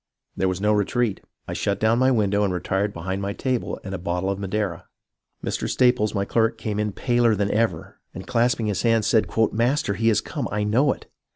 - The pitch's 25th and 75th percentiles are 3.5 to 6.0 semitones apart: No, average, 2.7 semitones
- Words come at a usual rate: No, fast, 215 wpm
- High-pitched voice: No, low, 105 Hz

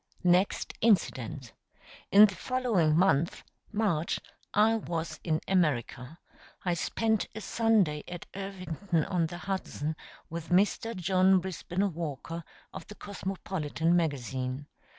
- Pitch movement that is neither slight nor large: Yes, average, 4.0 semitones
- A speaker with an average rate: No, slow, 115 wpm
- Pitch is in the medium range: Yes, medium, 175 Hz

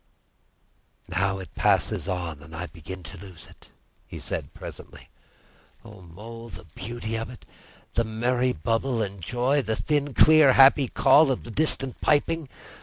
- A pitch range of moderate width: No, wide, 6.0 semitones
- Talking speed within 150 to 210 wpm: Yes, average, 155 wpm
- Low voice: Yes, low, 115 Hz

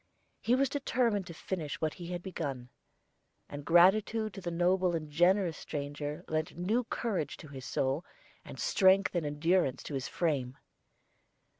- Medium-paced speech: Yes, average, 155 wpm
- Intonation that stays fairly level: No, average, 4.6 semitones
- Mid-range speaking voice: Yes, medium, 175 Hz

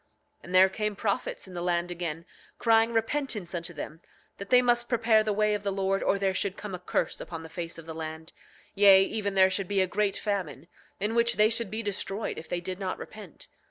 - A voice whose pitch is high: Yes, high, 195 Hz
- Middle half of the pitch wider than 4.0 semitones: No, average, 3.4 semitones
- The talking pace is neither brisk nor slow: No, fast, 230 wpm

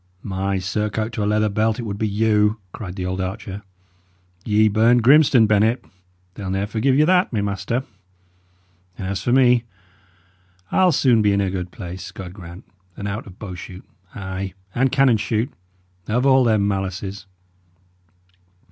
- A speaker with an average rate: Yes, average, 165 wpm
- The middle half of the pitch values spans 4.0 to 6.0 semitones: No, average, 3.1 semitones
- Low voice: Yes, low, 105 Hz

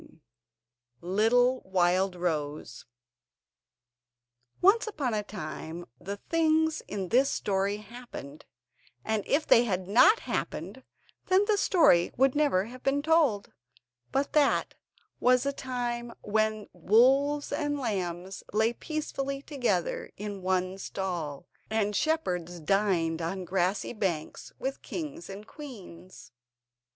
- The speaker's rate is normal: No, slow, 115 wpm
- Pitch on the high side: Yes, high, 210 Hz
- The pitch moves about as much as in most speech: No, wide, 6.9 semitones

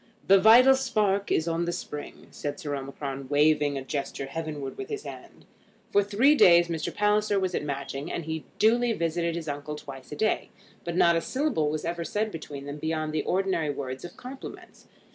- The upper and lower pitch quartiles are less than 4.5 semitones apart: No, wide, 5.6 semitones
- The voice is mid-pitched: Yes, medium, 165 Hz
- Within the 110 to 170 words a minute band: No, average, 195 wpm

